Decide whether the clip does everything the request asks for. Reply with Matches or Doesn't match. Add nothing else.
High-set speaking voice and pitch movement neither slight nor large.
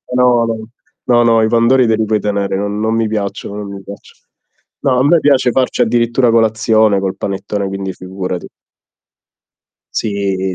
Doesn't match